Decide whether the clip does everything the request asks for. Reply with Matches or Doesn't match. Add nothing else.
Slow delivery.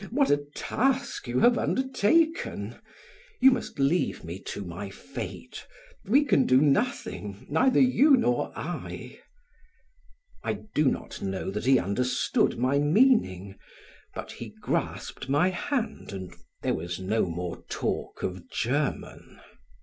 Matches